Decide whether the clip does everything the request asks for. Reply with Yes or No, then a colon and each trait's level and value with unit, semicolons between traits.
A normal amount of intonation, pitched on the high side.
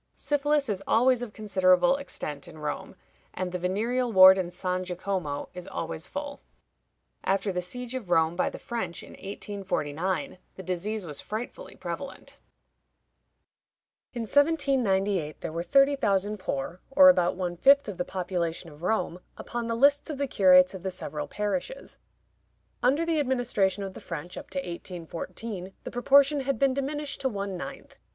No: wide, 6.5 semitones; high, 195 Hz